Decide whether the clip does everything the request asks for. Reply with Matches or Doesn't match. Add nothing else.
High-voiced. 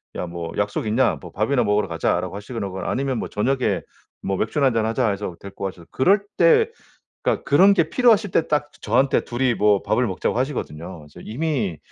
Doesn't match